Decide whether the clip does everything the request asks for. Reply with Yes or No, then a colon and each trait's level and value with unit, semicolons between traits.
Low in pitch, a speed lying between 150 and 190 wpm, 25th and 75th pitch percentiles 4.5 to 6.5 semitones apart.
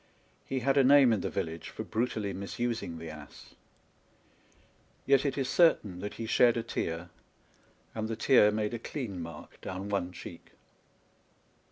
Yes: low, 110 Hz; average, 160 wpm; wide, 5.5 semitones